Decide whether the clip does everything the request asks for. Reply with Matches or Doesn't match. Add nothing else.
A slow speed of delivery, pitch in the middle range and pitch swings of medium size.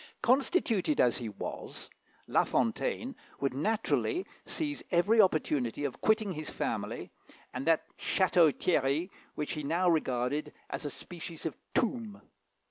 Doesn't match